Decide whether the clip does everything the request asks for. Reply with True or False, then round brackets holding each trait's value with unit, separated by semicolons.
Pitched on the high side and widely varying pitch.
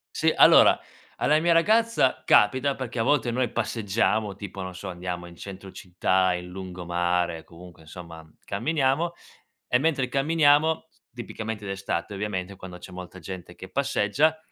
False (100 Hz; 6.8 semitones)